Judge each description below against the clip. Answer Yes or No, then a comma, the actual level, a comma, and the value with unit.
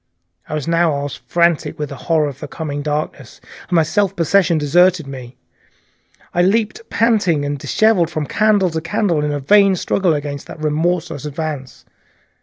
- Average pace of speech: Yes, average, 160 wpm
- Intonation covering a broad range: No, average, 3.7 semitones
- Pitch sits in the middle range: Yes, medium, 160 Hz